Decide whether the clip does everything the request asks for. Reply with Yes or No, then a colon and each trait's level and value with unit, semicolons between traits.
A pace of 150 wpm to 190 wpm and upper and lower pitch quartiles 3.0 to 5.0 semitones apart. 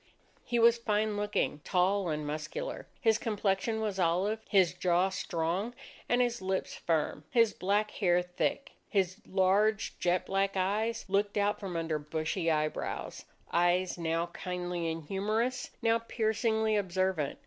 No: average, 140 wpm; average, 3.7 semitones